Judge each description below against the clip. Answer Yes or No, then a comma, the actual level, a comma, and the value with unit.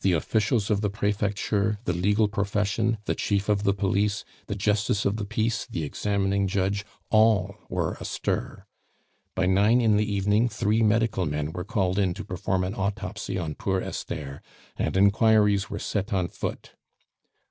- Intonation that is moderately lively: No, narrow, 1.9 semitones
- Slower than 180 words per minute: Yes, average, 165 wpm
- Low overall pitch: Yes, low, 100 Hz